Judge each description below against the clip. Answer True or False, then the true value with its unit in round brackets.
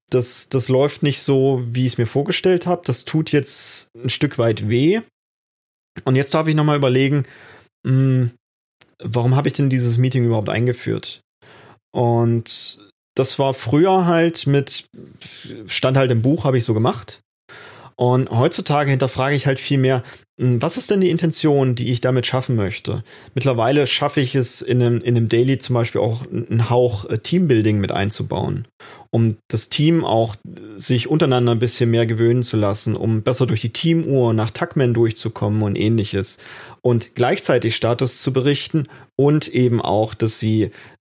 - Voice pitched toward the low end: True (125 Hz)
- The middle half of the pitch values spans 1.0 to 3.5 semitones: True (3.2 semitones)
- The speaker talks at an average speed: True (170 wpm)